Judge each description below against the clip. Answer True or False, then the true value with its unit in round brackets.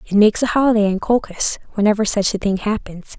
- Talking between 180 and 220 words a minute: True (205 wpm)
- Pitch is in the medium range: False (210 Hz)